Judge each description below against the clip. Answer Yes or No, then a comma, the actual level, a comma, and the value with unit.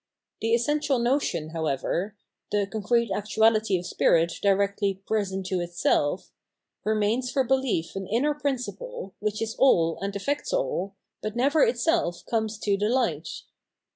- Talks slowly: No, average, 150 wpm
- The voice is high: Yes, high, 215 Hz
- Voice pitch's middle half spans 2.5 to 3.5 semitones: No, average, 4.5 semitones